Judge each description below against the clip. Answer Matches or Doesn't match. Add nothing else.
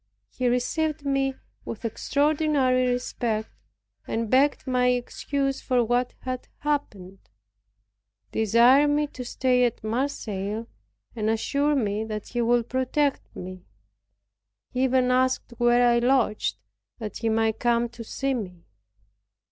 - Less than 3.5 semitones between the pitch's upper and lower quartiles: Matches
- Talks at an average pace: Doesn't match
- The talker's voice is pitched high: Matches